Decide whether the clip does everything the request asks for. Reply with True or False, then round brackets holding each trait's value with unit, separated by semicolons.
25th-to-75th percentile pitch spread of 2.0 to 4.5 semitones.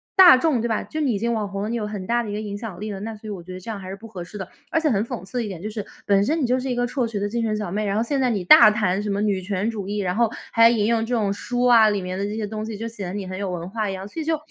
True (2.8 semitones)